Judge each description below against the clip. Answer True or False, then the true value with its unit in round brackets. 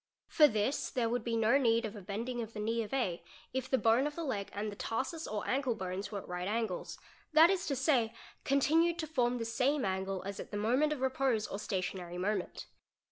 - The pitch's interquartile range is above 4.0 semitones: True (4.7 semitones)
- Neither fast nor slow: False (230 wpm)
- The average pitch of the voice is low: False (230 Hz)